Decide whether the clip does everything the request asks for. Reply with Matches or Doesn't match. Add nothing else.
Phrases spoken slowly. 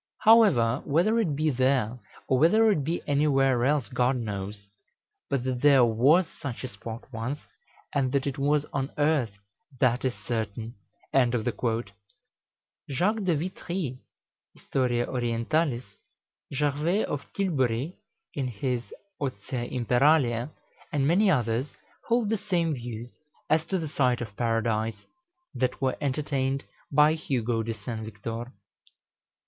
Matches